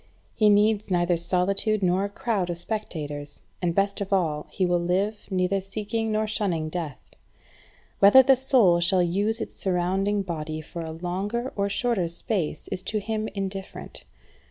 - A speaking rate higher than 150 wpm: Yes, average, 160 wpm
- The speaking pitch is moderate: No, high, 195 Hz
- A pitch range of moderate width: Yes, average, 3.4 semitones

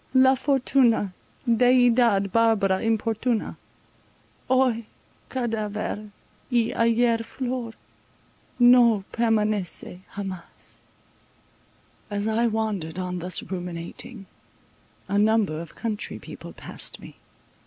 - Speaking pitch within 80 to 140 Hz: No, high, 225 Hz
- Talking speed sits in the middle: No, slow, 90 wpm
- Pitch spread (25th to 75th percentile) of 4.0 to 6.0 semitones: No, average, 3.2 semitones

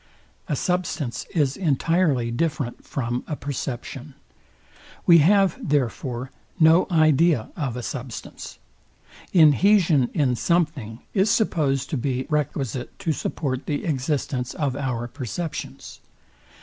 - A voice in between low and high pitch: Yes, medium, 145 Hz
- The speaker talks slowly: Yes, slow, 110 wpm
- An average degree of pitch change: Yes, average, 4.4 semitones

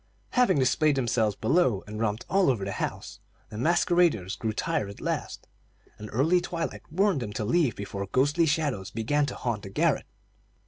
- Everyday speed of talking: Yes, average, 175 wpm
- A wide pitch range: Yes, wide, 7.7 semitones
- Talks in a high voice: No, low, 130 Hz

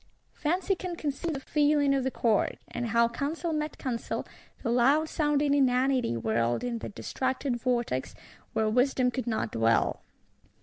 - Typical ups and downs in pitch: Yes, average, 4.0 semitones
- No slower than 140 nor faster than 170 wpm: Yes, average, 150 wpm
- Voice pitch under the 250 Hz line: No, very high, 260 Hz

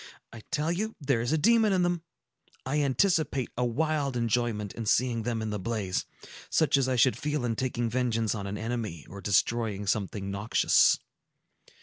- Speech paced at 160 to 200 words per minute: Yes, average, 180 wpm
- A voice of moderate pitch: No, low, 120 Hz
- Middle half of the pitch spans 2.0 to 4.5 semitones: No, average, 5.2 semitones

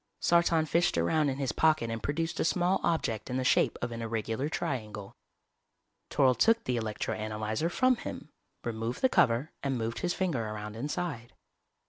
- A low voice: Yes, low, 130 Hz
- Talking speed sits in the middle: Yes, average, 170 wpm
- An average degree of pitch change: No, wide, 6.5 semitones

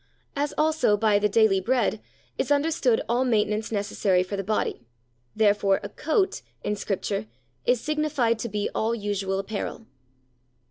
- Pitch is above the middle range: Yes, high, 220 Hz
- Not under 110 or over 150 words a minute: Yes, average, 145 wpm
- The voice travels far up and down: No, average, 3.8 semitones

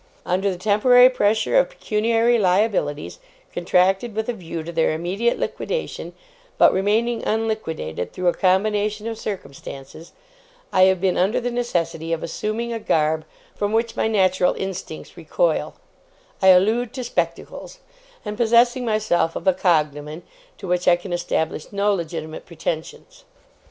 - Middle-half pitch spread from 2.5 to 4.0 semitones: No, average, 4.5 semitones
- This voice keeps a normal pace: Yes, average, 145 wpm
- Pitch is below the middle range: No, high, 195 Hz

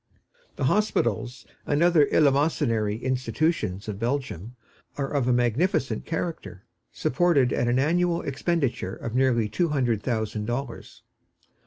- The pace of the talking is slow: Yes, slow, 125 wpm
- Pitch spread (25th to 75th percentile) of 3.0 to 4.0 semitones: No, average, 5.1 semitones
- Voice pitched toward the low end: Yes, low, 130 Hz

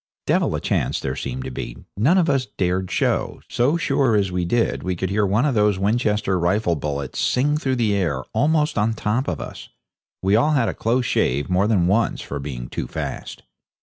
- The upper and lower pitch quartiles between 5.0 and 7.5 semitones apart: Yes, wide, 5.5 semitones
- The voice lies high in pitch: No, low, 105 Hz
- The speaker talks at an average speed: No, fast, 215 wpm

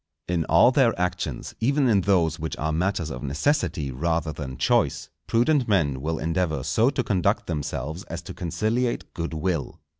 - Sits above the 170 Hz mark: No, very low, 85 Hz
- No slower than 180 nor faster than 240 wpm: No, average, 170 wpm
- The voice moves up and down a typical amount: No, wide, 5.7 semitones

